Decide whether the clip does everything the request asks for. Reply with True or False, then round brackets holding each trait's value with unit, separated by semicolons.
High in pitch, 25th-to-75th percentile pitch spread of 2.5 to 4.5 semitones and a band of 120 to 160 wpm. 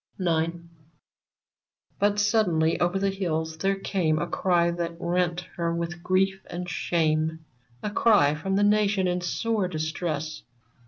False (175 Hz; 3.2 semitones; 145 wpm)